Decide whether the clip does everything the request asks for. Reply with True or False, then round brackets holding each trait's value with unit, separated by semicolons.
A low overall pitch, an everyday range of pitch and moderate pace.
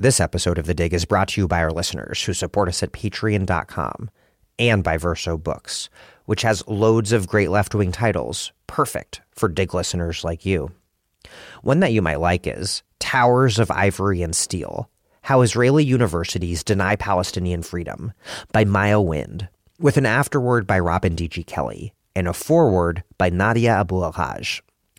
True (95 Hz; 3.9 semitones; 165 wpm)